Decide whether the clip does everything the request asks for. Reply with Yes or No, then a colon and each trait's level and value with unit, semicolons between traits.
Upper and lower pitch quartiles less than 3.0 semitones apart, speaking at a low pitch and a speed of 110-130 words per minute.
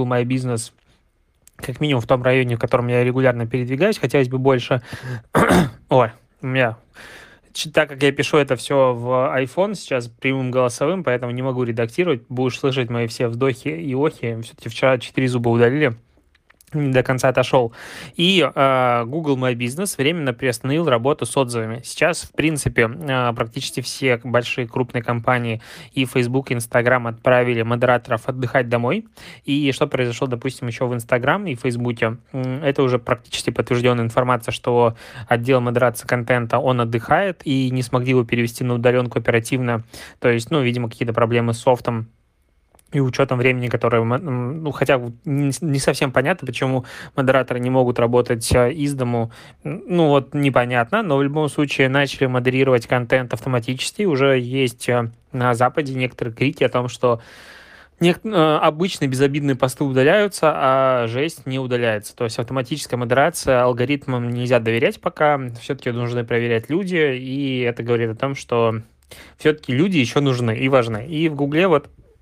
No: narrow, 2.4 semitones; low, 130 Hz; average, 155 wpm